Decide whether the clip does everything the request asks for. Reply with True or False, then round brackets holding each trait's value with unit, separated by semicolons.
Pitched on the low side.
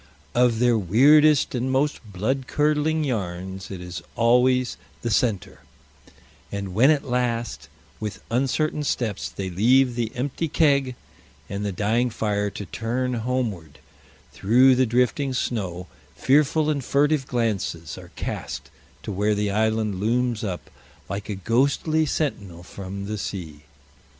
True (115 Hz)